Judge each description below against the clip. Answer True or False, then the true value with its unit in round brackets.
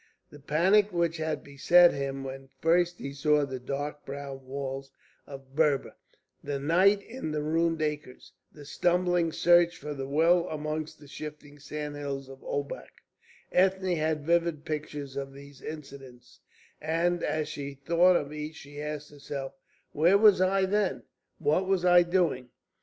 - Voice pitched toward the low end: False (150 Hz)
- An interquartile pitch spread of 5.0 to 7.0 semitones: False (3.5 semitones)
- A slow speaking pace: False (150 wpm)